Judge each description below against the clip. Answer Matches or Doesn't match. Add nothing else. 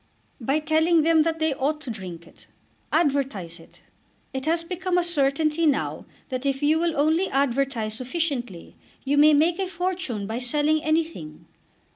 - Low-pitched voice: Doesn't match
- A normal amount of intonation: Matches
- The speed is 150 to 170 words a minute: Matches